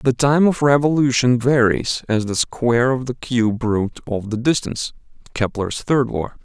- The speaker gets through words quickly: No, average, 170 wpm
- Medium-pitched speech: No, low, 125 Hz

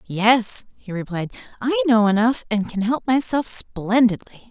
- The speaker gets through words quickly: No, average, 145 wpm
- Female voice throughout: Yes, female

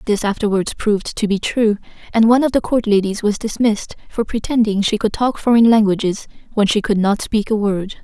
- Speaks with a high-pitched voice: Yes, high, 215 Hz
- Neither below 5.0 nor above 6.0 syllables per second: Yes, 5.6 syllables/s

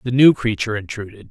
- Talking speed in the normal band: Yes, average, 185 wpm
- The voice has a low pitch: Yes, low, 110 Hz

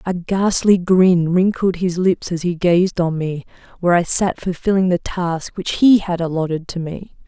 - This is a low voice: No, medium, 180 Hz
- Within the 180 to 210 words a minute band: Yes, average, 190 wpm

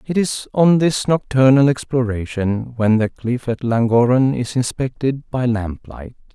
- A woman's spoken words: No, male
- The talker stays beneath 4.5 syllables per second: Yes, 4.2 syllables/s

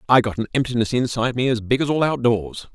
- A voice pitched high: No, low, 120 Hz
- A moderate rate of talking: No, fast, 240 wpm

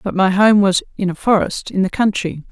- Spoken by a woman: Yes, female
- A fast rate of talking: Yes, fast, 240 wpm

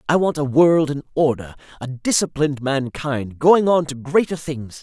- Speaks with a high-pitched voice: No, medium, 145 Hz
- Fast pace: No, average, 175 wpm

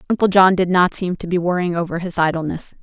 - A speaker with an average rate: No, fast, 235 wpm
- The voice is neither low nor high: Yes, medium, 175 Hz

